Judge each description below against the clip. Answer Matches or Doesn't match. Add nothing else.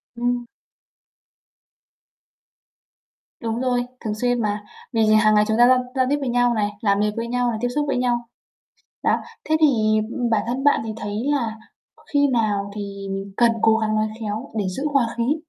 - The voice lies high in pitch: Matches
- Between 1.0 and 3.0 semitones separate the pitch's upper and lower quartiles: Matches